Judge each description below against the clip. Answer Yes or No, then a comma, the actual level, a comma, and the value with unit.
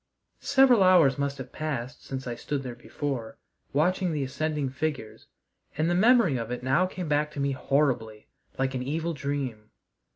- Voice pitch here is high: No, medium, 140 Hz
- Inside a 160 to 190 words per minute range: Yes, average, 170 wpm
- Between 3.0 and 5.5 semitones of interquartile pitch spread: Yes, average, 3.4 semitones